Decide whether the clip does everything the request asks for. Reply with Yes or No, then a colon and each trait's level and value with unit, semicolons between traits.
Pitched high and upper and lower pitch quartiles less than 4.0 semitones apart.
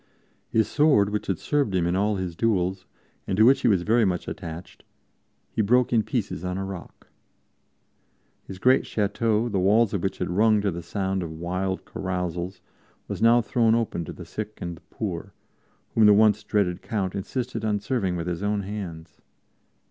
No: low, 100 Hz; average, 3.4 semitones